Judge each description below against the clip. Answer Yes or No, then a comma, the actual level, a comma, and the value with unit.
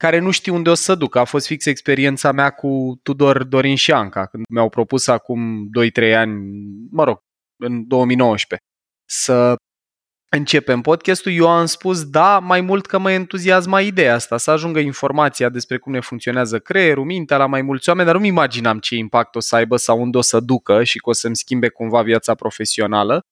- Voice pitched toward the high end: No, low, 130 Hz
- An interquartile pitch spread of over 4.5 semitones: Yes, average, 5.3 semitones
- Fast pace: Yes, fast, 195 wpm